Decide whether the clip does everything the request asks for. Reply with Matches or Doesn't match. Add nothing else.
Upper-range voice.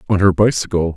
Doesn't match